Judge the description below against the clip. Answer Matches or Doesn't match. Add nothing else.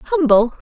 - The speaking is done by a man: Doesn't match